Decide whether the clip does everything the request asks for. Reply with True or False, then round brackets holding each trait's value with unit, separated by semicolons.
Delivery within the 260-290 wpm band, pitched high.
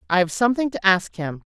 False (200 wpm; 200 Hz)